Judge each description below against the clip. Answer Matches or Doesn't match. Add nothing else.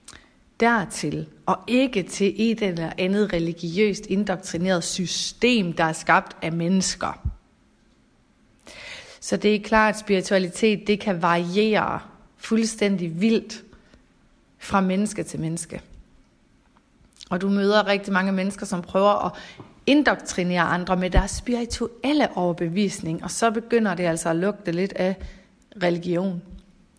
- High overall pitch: Matches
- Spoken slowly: Matches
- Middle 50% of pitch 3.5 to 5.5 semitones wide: Doesn't match